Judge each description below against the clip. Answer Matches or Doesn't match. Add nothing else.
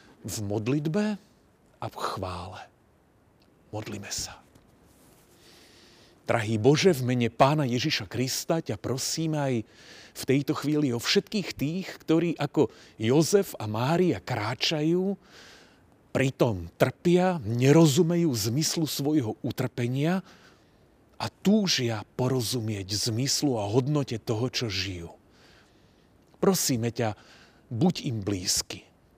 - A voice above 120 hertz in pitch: Matches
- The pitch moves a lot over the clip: Matches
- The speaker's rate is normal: Doesn't match